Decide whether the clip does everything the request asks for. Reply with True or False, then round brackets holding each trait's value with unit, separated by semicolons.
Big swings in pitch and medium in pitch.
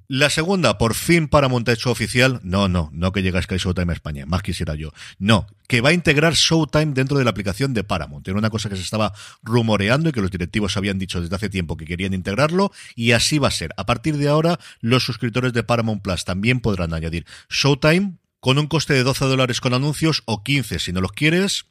False (6.7 semitones; 115 Hz)